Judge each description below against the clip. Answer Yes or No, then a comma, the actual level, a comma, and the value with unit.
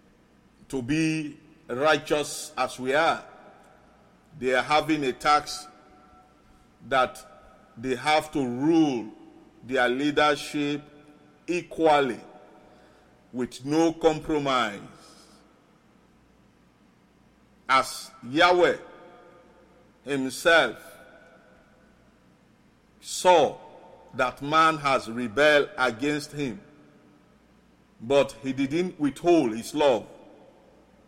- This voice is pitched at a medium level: Yes, medium, 150 Hz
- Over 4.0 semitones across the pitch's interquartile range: No, average, 3.3 semitones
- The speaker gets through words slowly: Yes, slow, 75 wpm